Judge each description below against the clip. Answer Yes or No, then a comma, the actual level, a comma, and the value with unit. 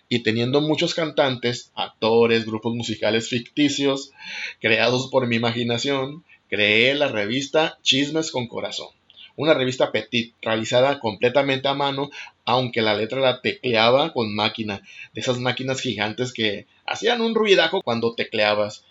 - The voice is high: No, low, 125 Hz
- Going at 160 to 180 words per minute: No, average, 135 wpm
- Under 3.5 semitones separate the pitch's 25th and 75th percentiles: No, average, 3.8 semitones